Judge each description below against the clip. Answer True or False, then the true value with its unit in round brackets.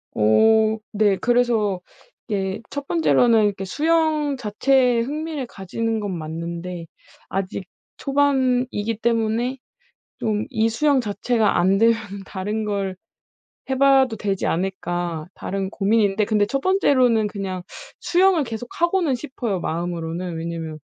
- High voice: True (220 Hz)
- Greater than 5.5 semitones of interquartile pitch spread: False (5.1 semitones)